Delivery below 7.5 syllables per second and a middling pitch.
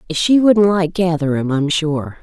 Yes: 4.0 syllables/s; medium, 170 Hz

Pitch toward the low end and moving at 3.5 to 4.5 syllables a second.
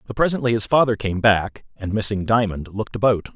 No: low, 105 Hz; 5.9 syllables/s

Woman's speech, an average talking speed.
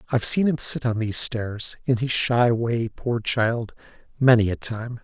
No: male; average, 190 wpm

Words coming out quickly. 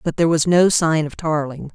Yes: fast, 240 wpm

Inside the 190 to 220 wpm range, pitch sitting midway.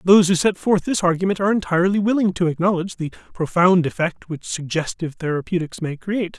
No: average, 180 wpm; medium, 180 Hz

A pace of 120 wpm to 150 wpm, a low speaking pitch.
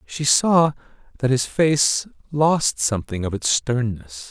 Yes: average, 140 wpm; low, 130 Hz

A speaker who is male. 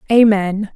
No: female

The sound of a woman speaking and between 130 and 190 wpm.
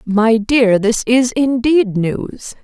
Yes: female; slow, 135 wpm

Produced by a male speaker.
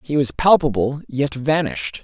Yes: male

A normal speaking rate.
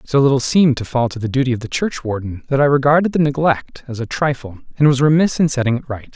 No: fast, 255 wpm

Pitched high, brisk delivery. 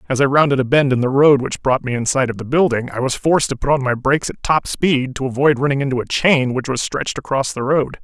No: low, 135 Hz; fast, 290 wpm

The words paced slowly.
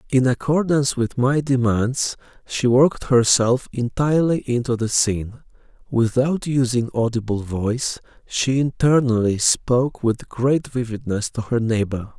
Yes: slow, 125 wpm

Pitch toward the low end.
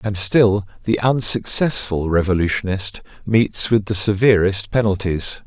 Yes: low, 105 Hz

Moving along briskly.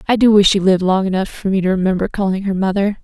Yes: fast, 275 wpm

